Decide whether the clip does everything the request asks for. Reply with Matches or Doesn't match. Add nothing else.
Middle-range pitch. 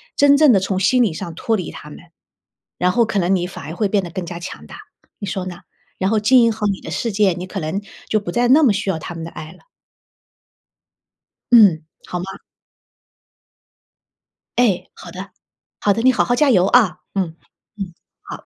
Doesn't match